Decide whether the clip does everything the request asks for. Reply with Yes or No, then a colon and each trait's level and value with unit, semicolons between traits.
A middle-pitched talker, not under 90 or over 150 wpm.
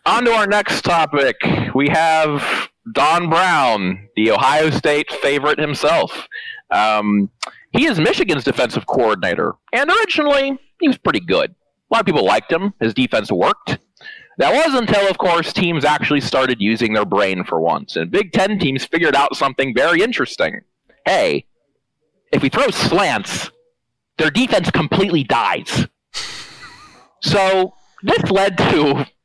Yes: medium, 170 Hz; average, 145 wpm